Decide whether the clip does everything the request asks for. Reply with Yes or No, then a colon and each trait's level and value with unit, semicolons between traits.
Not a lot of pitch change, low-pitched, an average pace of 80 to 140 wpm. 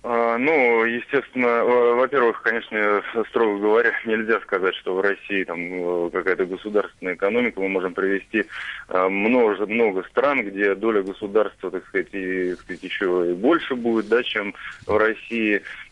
No: average, 3.5 semitones; low, 105 Hz; average, 135 wpm